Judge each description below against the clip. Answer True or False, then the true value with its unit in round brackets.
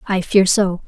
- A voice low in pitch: False (190 Hz)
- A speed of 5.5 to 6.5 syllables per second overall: False (4.0 syllables/s)